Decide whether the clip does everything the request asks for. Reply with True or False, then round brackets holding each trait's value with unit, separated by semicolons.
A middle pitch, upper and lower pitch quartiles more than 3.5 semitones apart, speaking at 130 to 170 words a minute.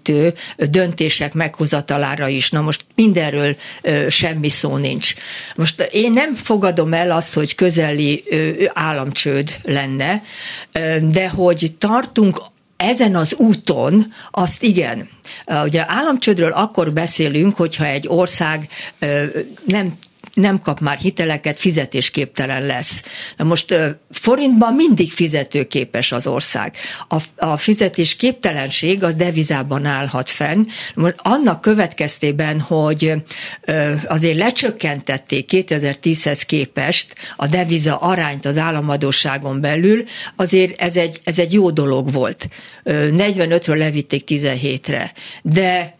False (165 Hz; 3.9 semitones; 105 wpm)